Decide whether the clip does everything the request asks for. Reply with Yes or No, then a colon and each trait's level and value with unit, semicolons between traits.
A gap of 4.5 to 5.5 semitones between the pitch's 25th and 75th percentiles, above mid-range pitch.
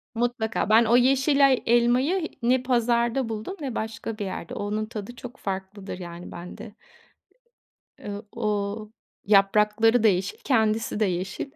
No: average, 3.1 semitones; high, 225 Hz